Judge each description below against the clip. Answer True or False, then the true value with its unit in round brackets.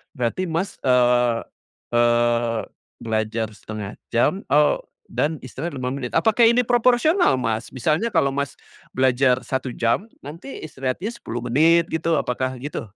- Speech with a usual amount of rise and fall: False (5.8 semitones)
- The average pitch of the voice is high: False (130 Hz)